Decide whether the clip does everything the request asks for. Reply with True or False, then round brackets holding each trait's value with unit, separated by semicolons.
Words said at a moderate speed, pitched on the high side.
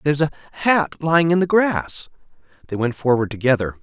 False (190 wpm; 145 Hz)